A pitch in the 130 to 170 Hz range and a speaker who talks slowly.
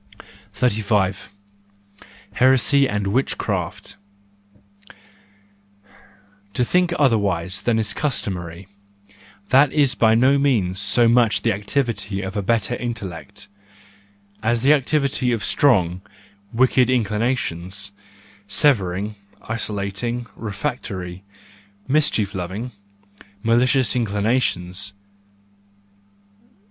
No: low, 110 Hz; slow, 80 wpm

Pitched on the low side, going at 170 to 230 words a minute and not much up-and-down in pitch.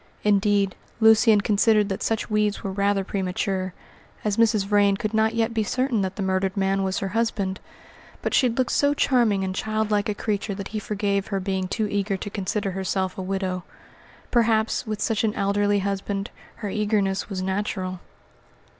No: high, 205 Hz; average, 175 wpm; narrow, 2.0 semitones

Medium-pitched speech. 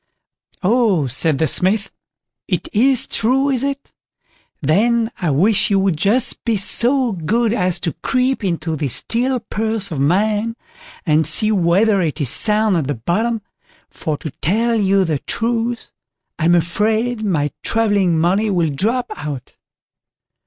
No: high, 205 Hz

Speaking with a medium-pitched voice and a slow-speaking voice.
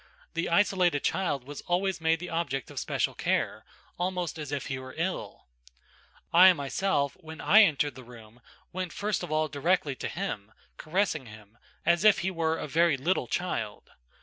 No: medium, 165 Hz; average, 175 wpm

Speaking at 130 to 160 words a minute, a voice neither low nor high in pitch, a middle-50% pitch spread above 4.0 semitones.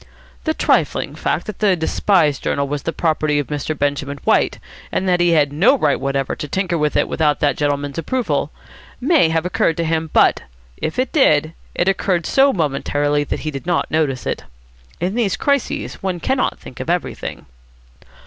No: average, 185 wpm; medium, 160 Hz; average, 4.4 semitones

